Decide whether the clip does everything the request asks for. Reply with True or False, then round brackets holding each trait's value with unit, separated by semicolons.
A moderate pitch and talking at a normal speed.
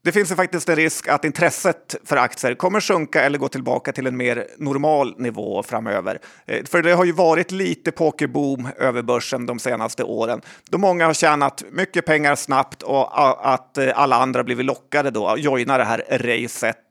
True (145 Hz; 185 wpm)